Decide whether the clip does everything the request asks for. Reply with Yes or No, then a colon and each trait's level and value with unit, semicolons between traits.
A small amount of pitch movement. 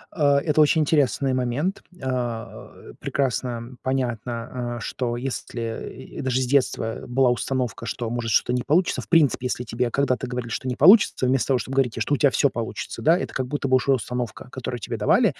Yes: narrow, 2.2 semitones